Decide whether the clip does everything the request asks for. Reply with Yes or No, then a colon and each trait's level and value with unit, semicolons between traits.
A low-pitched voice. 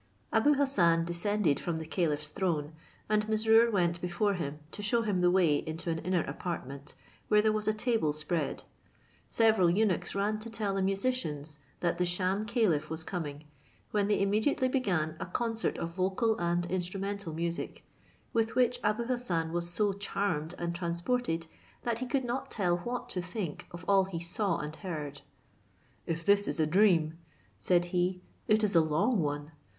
No: medium, 185 Hz